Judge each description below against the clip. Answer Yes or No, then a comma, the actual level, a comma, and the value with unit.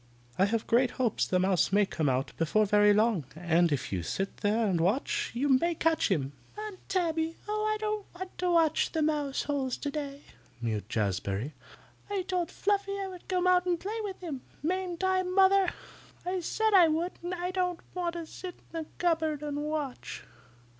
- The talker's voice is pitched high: Yes, very high, 320 Hz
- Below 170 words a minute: No, average, 195 wpm